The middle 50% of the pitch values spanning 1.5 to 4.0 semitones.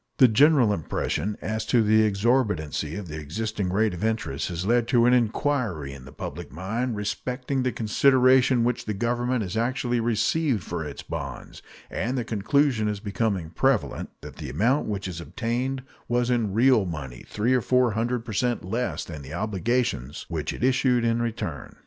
No: average, 4.6 semitones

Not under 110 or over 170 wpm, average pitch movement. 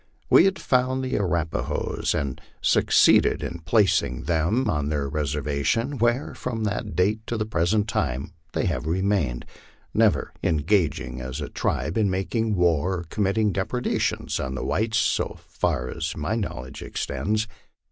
No: average, 155 wpm; wide, 6.7 semitones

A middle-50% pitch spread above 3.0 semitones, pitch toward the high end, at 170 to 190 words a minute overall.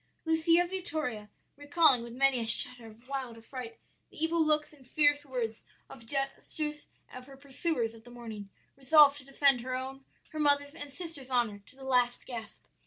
Yes: average, 3.6 semitones; very high, 270 Hz; average, 175 wpm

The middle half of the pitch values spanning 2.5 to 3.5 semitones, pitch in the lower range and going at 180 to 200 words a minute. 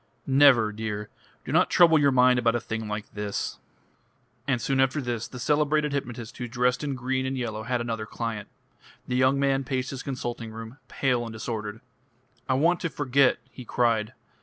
Yes: average, 3.2 semitones; low, 125 Hz; average, 185 wpm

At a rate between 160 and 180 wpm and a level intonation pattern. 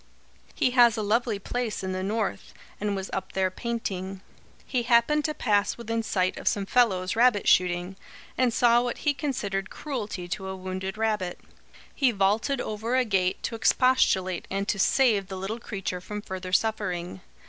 No: average, 170 wpm; average, 3.8 semitones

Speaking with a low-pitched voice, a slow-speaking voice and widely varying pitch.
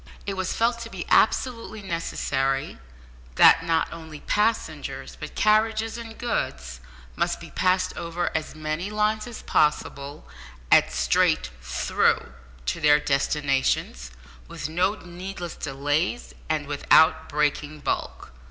No: medium, 165 Hz; slow, 125 wpm; wide, 6.5 semitones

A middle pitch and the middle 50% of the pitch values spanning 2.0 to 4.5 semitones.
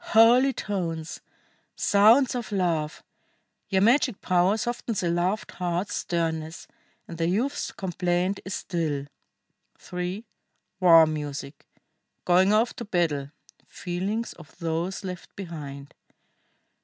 Yes: medium, 180 Hz; average, 3.9 semitones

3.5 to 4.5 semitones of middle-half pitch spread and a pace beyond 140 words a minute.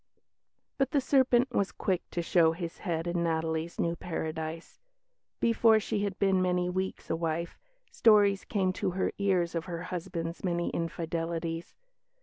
No: average, 2.9 semitones; average, 150 wpm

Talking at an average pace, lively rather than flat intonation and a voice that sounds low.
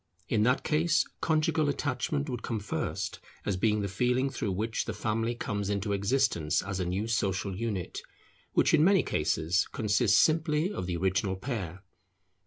Yes: average, 165 wpm; wide, 5.7 semitones; low, 105 Hz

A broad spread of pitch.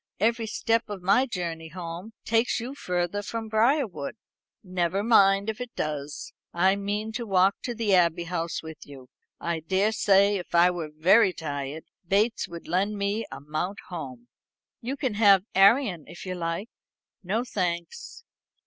No: average, 4.3 semitones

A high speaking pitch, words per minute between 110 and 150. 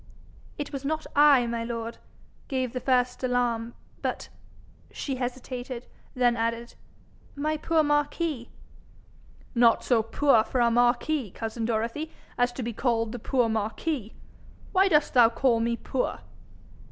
Yes: high, 245 Hz; average, 140 wpm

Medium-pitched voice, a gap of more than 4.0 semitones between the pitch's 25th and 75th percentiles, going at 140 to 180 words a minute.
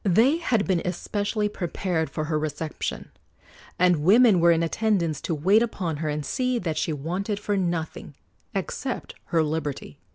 Yes: medium, 175 Hz; average, 4.5 semitones; average, 160 wpm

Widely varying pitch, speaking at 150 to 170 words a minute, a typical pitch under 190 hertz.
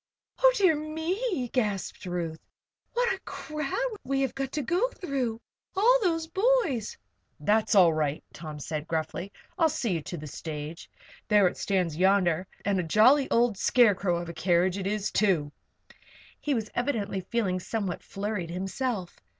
No: wide, 8.4 semitones; average, 160 wpm; high, 210 Hz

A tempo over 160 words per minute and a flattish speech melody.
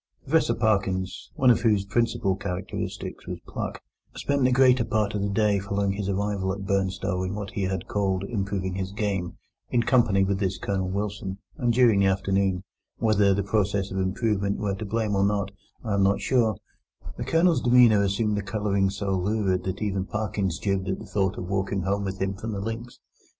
Yes: average, 190 wpm; narrow, 1.8 semitones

